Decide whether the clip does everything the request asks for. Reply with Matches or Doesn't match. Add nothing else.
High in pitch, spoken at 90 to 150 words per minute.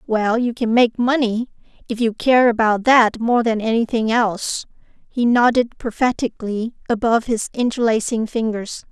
Matches